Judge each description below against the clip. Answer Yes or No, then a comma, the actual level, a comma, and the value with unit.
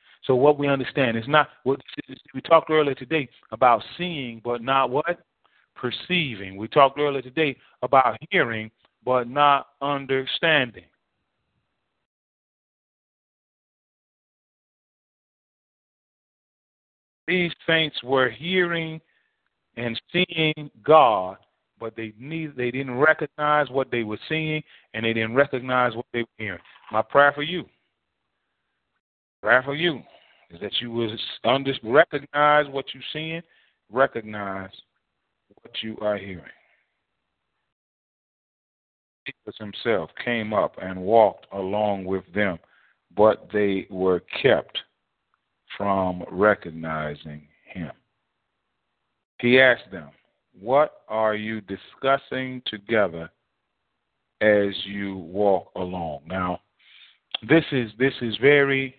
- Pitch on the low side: Yes, low, 125 Hz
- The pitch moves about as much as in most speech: No, wide, 5.7 semitones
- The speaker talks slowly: Yes, slow, 105 wpm